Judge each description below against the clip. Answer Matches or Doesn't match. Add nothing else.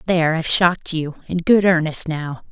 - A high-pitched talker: Doesn't match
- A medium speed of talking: Matches